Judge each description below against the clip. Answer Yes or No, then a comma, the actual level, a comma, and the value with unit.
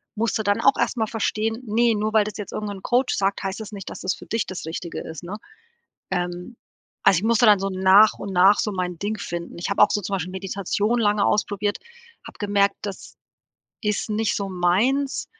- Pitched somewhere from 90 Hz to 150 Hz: No, high, 205 Hz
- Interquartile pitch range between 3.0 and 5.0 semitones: No, narrow, 2.4 semitones